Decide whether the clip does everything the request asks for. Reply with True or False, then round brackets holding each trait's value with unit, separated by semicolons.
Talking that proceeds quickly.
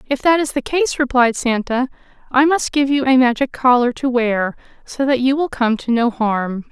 True (215 wpm)